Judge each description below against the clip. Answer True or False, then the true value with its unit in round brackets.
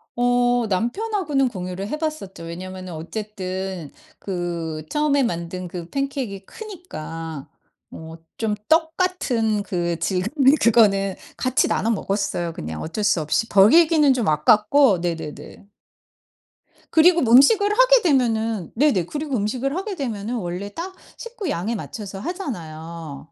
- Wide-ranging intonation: True (8.0 semitones)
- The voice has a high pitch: True (215 Hz)